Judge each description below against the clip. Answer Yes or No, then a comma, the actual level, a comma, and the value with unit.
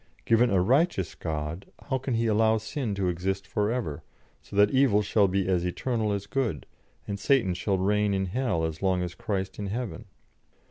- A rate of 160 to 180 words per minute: No, average, 190 wpm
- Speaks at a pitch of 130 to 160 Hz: No, low, 100 Hz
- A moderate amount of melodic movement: Yes, average, 3.5 semitones